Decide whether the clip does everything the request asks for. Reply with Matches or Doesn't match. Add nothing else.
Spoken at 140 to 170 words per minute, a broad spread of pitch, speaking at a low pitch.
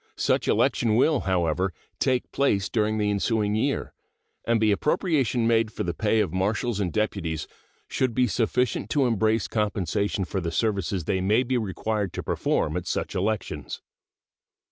Doesn't match